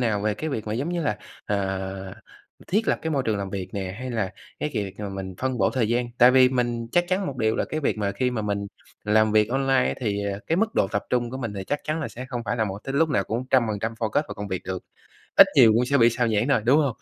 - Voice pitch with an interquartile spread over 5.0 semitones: No, average, 4.4 semitones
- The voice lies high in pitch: No, low, 115 Hz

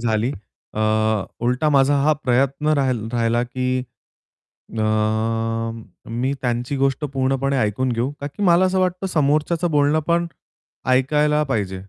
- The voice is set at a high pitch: No, low, 135 Hz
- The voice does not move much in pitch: No, average, 3.7 semitones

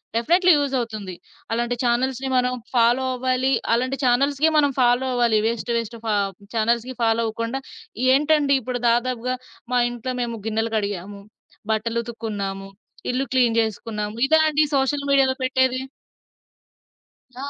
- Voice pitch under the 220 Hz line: No, high, 245 Hz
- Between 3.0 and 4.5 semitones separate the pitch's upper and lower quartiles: No, narrow, 2.5 semitones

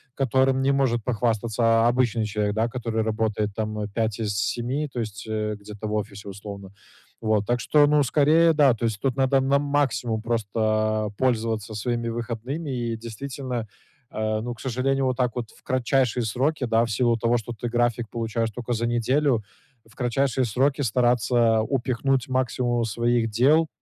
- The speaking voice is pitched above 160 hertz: No, low, 120 Hz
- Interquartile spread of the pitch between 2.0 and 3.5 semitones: Yes, average, 3.0 semitones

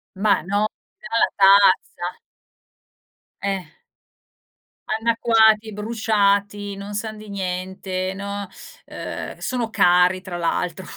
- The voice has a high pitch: Yes, high, 200 Hz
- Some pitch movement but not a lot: No, narrow, 2.3 semitones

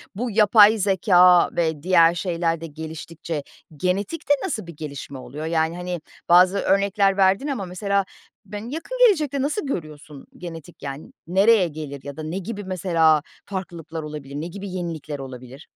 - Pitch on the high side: No, medium, 175 Hz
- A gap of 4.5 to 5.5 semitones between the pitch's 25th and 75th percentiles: No, average, 4.1 semitones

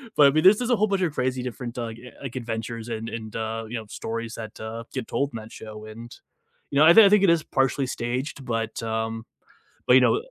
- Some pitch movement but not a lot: Yes, average, 3.8 semitones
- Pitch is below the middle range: Yes, low, 120 Hz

